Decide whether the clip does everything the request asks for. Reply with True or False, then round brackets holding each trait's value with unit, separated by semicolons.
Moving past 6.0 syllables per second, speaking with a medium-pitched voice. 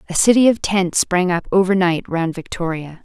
False (5.0 syllables/s; 180 Hz)